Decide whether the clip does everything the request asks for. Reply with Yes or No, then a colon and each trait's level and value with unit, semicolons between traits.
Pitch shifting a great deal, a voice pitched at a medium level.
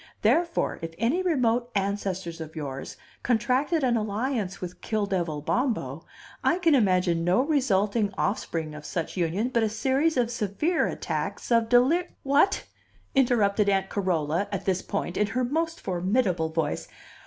No: wide, 6.0 semitones; high, 210 Hz